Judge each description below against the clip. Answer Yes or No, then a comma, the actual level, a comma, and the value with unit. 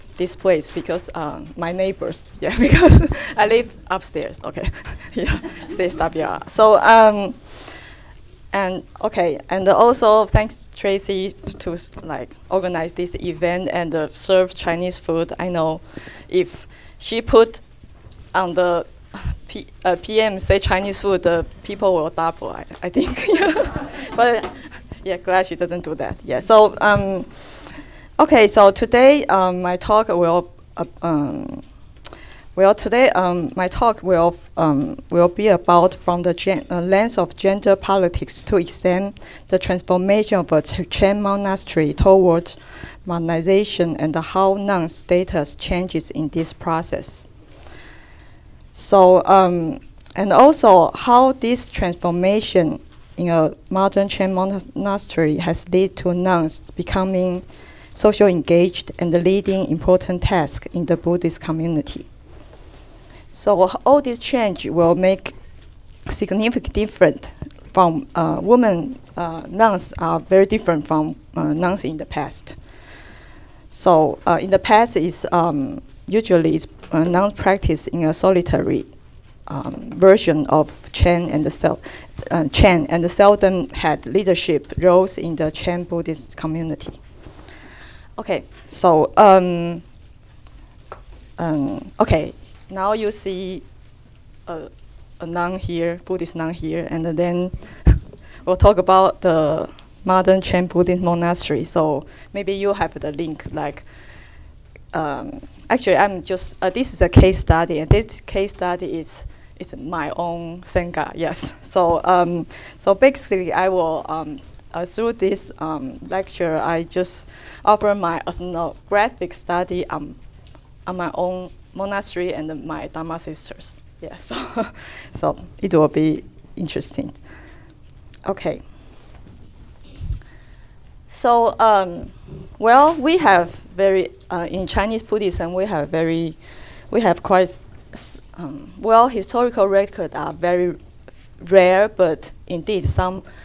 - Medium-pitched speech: Yes, medium, 180 Hz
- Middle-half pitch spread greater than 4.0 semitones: No, average, 2.9 semitones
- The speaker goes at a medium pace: No, slow, 130 wpm